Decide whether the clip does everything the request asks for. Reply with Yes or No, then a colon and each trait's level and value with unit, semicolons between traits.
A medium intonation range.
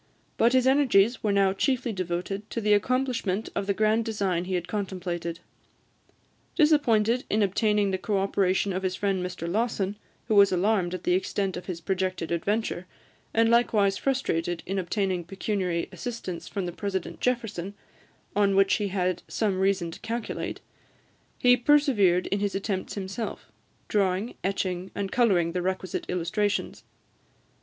Yes: average, 3.0 semitones